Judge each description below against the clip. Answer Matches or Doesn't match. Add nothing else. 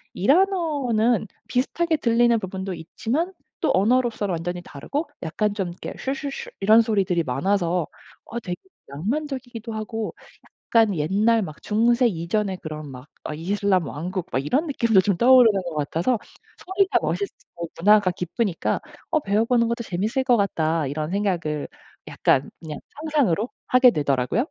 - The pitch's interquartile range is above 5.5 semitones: Matches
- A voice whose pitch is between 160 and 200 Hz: Doesn't match